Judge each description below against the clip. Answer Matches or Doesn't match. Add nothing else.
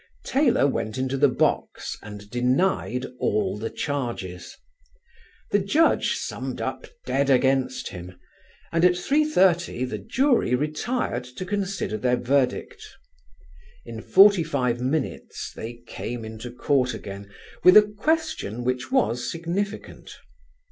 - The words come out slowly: Matches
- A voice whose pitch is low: Matches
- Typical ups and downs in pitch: Doesn't match